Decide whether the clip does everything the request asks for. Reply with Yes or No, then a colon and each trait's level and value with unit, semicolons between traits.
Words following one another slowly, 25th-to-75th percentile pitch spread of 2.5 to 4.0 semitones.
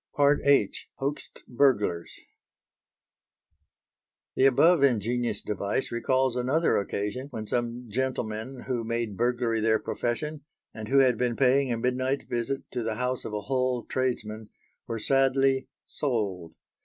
Yes: slow, 130 wpm; average, 3.0 semitones